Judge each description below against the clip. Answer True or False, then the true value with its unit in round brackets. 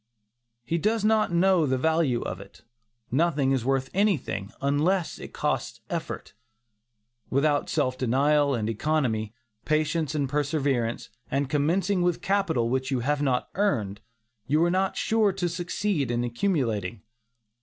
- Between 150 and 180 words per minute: False (140 wpm)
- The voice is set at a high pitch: False (145 Hz)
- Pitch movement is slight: False (5.3 semitones)